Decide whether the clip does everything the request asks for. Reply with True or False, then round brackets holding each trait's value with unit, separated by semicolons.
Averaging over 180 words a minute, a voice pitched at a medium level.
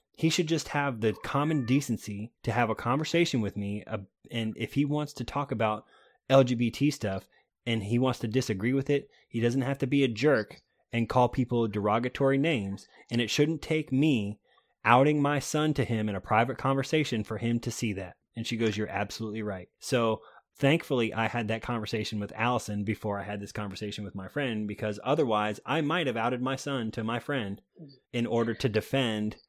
False (200 wpm; 120 Hz)